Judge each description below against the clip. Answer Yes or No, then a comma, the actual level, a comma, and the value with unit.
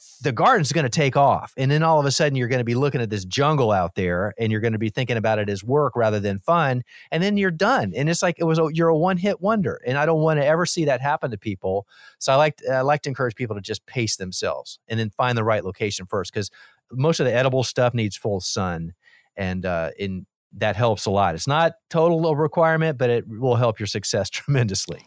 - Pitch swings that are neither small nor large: No, wide, 6.7 semitones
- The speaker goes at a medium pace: No, fast, 255 wpm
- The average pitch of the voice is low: Yes, low, 125 Hz